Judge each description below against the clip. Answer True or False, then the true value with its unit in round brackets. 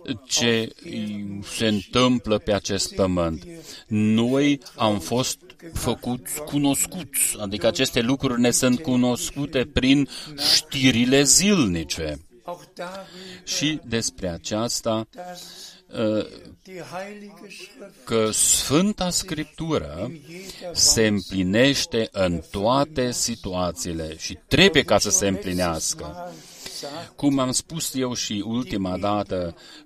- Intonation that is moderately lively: False (6.5 semitones)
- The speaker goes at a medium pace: False (90 wpm)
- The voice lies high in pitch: False (125 Hz)